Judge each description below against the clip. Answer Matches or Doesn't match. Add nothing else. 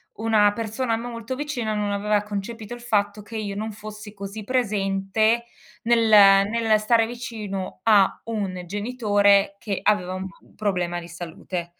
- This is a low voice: Doesn't match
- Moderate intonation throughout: Doesn't match